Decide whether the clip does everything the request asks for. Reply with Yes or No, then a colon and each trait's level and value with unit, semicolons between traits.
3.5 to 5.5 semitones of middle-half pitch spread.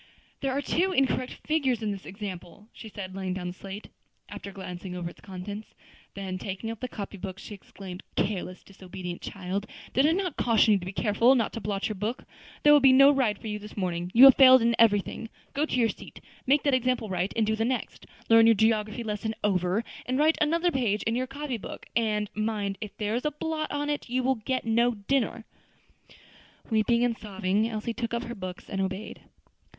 Yes: average, 4.5 semitones